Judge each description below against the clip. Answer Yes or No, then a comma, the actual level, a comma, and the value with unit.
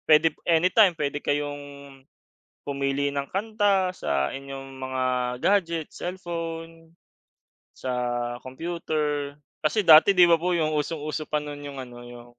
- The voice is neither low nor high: Yes, medium, 155 Hz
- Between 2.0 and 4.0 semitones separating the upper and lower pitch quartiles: Yes, average, 3.4 semitones